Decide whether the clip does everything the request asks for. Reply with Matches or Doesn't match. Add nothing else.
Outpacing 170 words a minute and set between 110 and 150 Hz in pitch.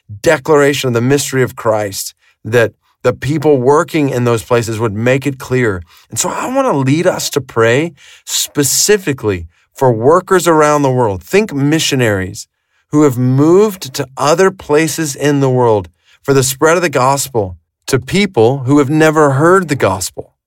Doesn't match